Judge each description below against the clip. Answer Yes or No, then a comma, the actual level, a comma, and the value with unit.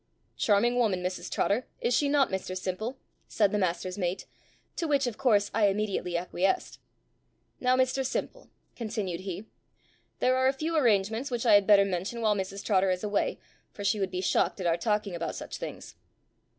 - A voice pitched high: Yes, high, 205 Hz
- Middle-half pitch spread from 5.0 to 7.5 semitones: No, average, 4.5 semitones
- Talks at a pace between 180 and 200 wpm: Yes, average, 185 wpm